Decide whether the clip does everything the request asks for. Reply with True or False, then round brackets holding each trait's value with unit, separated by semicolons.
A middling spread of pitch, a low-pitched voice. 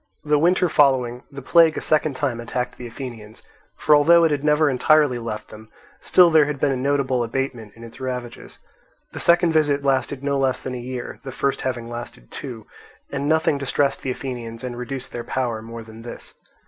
True (3.3 semitones; 130 Hz)